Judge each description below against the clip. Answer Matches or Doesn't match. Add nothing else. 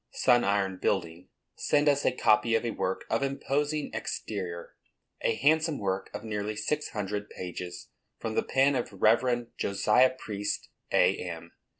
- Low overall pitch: Matches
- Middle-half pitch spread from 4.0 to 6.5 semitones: Matches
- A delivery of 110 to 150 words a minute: Matches